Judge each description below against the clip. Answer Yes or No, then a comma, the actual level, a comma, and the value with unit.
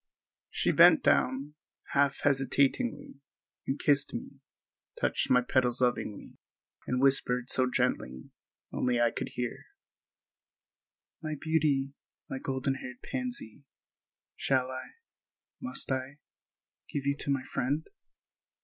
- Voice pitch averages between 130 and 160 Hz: Yes, low, 135 Hz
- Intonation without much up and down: Yes, narrow, 2.1 semitones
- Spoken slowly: Yes, slow, 105 wpm